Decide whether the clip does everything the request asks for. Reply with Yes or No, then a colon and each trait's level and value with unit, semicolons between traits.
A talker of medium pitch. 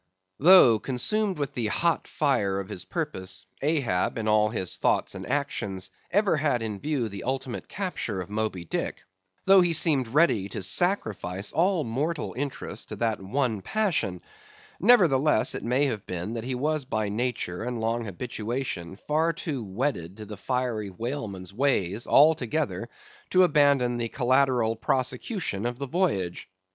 No: low, 125 Hz